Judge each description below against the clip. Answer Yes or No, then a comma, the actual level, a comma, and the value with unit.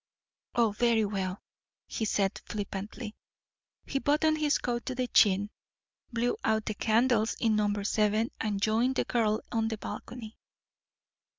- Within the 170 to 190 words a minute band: No, average, 140 wpm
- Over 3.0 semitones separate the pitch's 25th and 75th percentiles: No, narrow, 2.5 semitones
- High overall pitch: Yes, high, 220 Hz